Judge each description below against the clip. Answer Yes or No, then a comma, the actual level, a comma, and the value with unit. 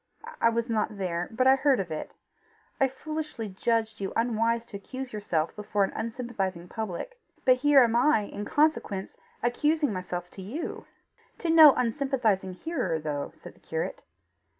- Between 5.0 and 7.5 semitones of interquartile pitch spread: Yes, wide, 5.6 semitones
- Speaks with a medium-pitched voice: No, high, 230 Hz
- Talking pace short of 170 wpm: Yes, average, 160 wpm